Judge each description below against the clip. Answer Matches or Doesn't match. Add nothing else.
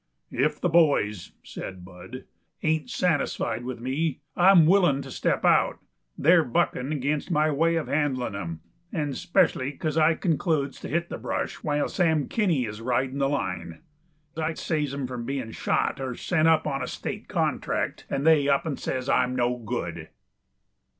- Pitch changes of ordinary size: Matches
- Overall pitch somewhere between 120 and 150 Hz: Matches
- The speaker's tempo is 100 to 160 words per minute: Doesn't match